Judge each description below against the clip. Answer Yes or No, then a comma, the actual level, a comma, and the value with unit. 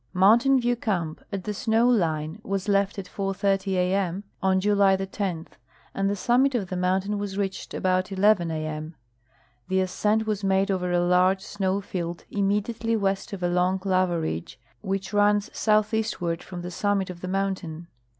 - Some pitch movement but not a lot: No, narrow, 2.2 semitones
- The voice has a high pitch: Yes, high, 195 Hz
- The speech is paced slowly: No, average, 175 wpm